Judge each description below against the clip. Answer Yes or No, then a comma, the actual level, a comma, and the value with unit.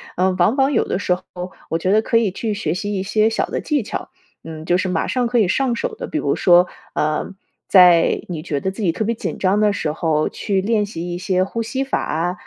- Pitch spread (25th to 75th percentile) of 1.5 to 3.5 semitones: No, average, 4.1 semitones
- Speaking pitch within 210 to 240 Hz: No, high, 190 Hz